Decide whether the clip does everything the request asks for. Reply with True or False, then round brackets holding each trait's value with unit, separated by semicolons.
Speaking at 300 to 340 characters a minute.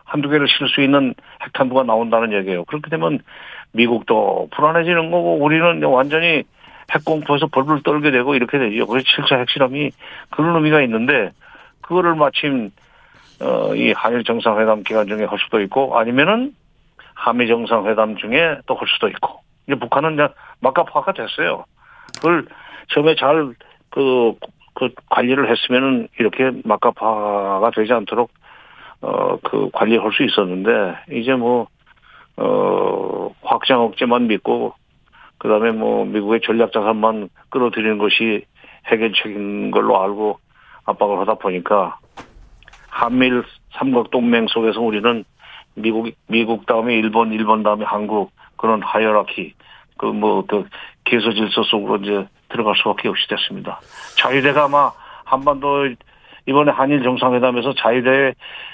True (305 characters per minute)